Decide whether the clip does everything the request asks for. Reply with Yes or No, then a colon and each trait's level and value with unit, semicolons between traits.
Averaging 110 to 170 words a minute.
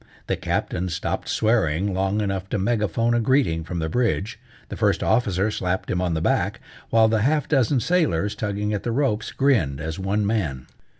No: average, 185 wpm